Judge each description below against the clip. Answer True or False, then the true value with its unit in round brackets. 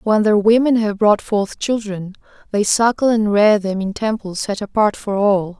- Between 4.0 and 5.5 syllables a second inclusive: True (4.4 syllables/s)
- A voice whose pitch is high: True (210 Hz)